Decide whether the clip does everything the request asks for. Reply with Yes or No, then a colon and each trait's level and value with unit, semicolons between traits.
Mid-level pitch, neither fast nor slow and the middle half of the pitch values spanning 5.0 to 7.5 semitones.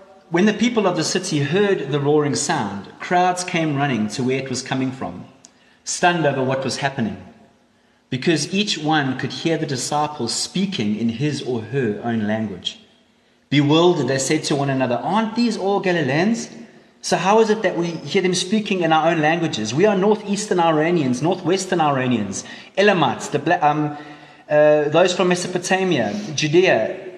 Yes: medium, 160 Hz; average, 160 wpm; wide, 5.5 semitones